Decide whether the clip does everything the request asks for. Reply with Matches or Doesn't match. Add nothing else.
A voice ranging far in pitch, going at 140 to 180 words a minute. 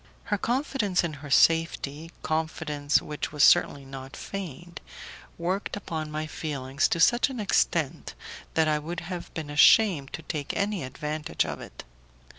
Doesn't match